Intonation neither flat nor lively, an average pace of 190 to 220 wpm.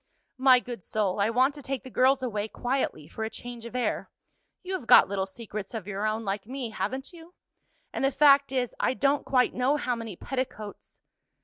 Yes: average, 3.8 semitones; average, 200 wpm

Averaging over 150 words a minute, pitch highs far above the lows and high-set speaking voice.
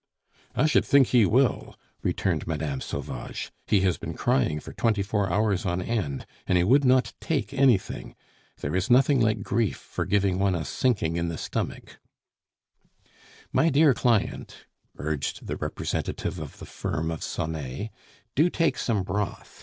No: average, 160 wpm; wide, 7.0 semitones; low, 100 Hz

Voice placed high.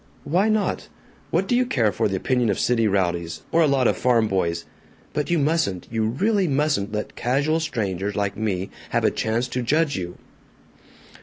No: low, 120 Hz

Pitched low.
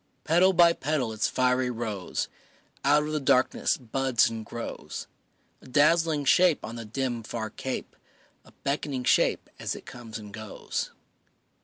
Yes: low, 130 Hz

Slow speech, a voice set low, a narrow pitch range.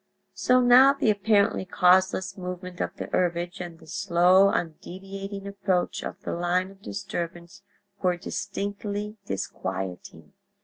No: slow, 125 wpm; high, 190 Hz; narrow, 2.2 semitones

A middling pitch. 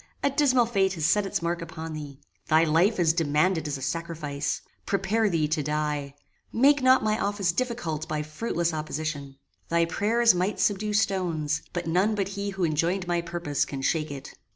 Yes: medium, 170 Hz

